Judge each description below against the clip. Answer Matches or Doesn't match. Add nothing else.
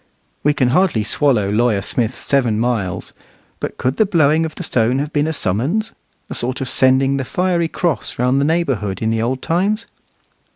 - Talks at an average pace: Matches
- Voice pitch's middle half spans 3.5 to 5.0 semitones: Doesn't match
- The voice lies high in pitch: Doesn't match